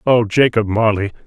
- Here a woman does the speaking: No, male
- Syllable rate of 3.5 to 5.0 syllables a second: Yes, 4.9 syllables/s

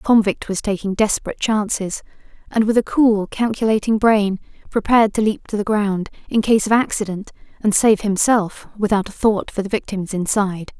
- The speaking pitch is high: Yes, high, 210 Hz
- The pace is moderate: Yes, average, 180 wpm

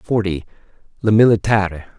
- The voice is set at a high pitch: No, low, 100 Hz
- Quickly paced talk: No, slow, 90 wpm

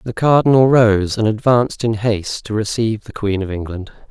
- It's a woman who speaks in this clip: No, male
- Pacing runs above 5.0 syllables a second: Yes, 5.5 syllables/s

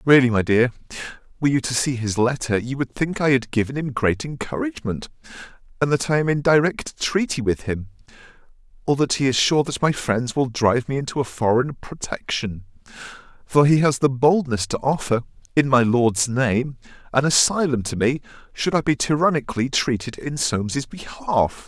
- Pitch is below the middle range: Yes, low, 130 Hz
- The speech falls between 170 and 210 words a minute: Yes, average, 180 wpm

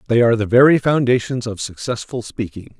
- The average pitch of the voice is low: Yes, low, 120 Hz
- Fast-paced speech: No, average, 170 wpm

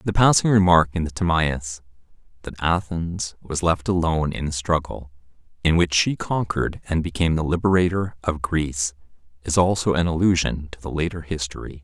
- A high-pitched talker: No, very low, 85 Hz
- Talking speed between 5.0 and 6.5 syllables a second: Yes, 5.4 syllables/s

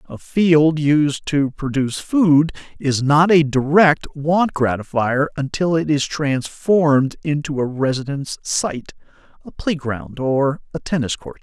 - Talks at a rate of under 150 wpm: Yes, slow, 135 wpm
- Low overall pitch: No, medium, 145 Hz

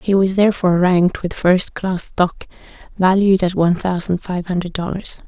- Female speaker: Yes, female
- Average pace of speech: Yes, average, 160 wpm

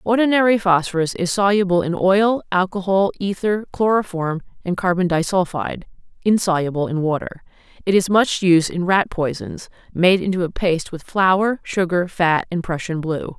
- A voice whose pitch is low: No, medium, 185 Hz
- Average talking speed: Yes, average, 150 wpm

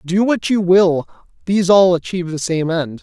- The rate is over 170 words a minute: Yes, average, 200 wpm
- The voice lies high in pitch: No, medium, 180 Hz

